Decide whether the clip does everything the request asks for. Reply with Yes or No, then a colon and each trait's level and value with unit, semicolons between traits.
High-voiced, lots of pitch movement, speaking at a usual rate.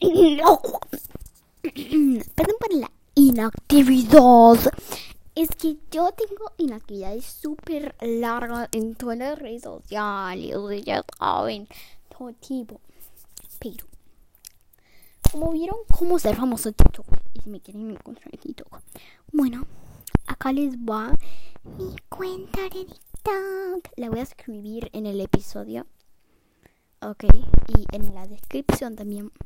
No: high, 245 Hz; wide, 6.8 semitones; slow, 115 wpm